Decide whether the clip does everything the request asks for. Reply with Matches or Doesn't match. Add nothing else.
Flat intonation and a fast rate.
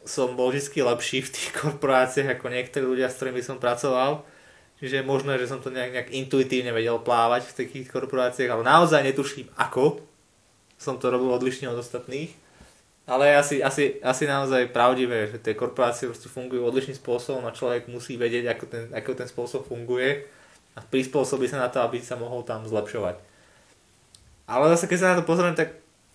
Matches